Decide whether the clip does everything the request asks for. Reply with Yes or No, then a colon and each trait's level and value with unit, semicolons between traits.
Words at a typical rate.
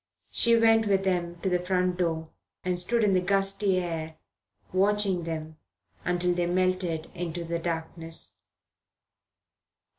No: slow, 130 wpm